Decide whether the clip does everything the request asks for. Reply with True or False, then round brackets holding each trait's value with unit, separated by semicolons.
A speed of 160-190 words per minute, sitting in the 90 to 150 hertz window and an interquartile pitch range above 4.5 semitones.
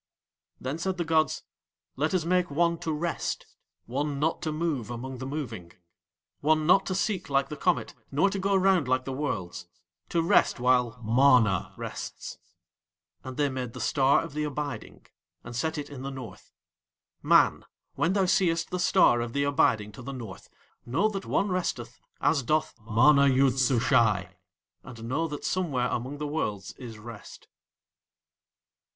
True (165 wpm; 140 Hz; 4.9 semitones)